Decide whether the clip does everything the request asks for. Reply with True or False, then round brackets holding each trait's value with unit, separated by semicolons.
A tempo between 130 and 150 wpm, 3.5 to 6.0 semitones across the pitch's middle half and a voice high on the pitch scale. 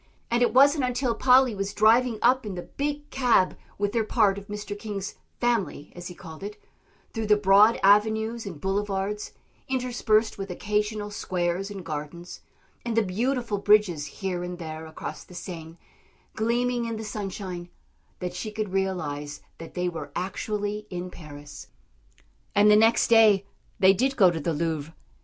False (165 wpm; 3.9 semitones; 205 Hz)